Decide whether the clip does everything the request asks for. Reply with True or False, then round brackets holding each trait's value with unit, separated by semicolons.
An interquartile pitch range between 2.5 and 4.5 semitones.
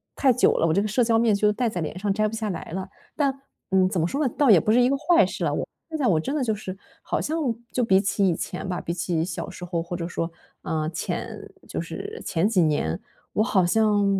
False (5.1 semitones)